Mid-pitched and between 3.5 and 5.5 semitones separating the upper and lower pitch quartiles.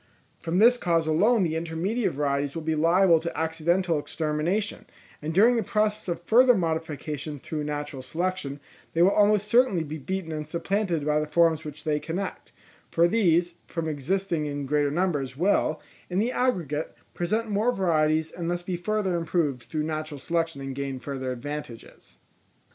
Yes: medium, 165 Hz; average, 3.9 semitones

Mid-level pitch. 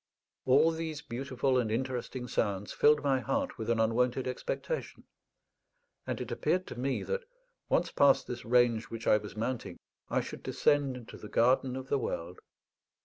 No: low, 125 Hz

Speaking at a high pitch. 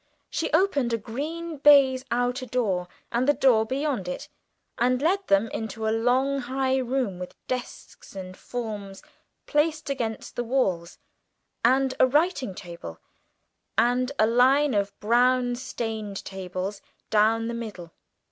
Yes: high, 245 Hz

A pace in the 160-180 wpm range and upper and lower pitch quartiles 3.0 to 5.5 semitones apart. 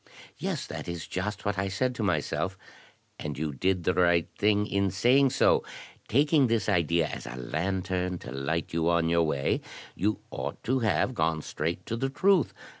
Yes: average, 175 wpm; average, 4.7 semitones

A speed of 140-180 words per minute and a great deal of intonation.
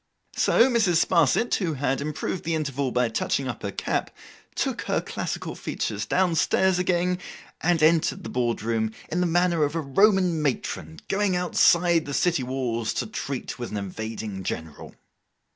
Yes: average, 165 wpm; wide, 6.5 semitones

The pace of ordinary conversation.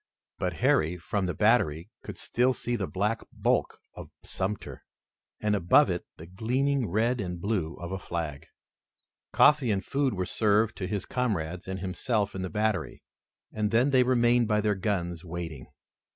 Yes: average, 165 wpm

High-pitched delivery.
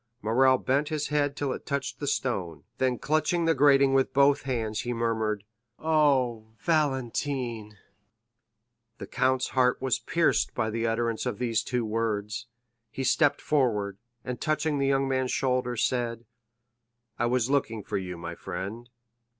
No: low, 125 Hz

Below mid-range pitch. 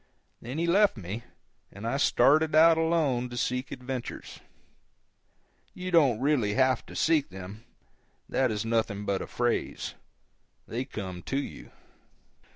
Yes: low, 125 Hz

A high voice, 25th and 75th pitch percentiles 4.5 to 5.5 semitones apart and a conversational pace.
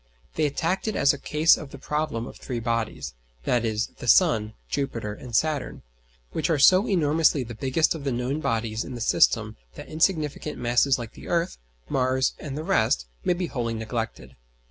No: low, 135 Hz; average, 5.1 semitones; average, 185 wpm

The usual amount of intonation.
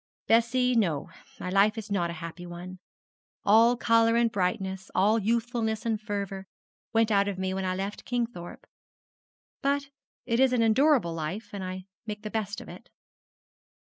Yes: average, 3.6 semitones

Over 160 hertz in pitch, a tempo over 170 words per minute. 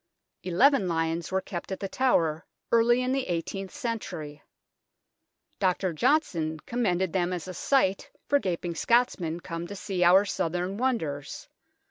No: medium, 185 Hz; average, 145 wpm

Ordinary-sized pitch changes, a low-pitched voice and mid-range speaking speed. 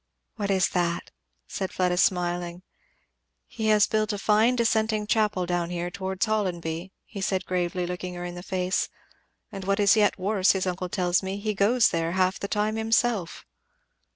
No: average, 3.0 semitones; high, 190 Hz; average, 175 wpm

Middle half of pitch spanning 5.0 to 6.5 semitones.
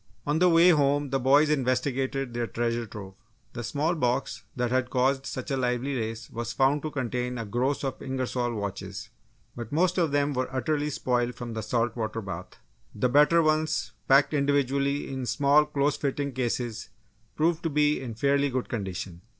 No: average, 3.3 semitones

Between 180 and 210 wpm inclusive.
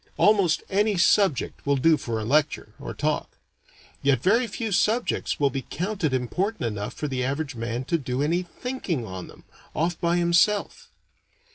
No: average, 165 wpm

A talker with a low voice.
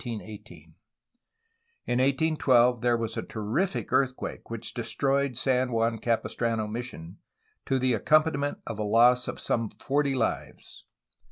Yes: low, 120 Hz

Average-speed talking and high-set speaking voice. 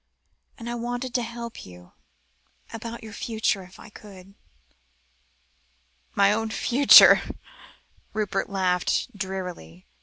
No: slow, 115 wpm; high, 210 Hz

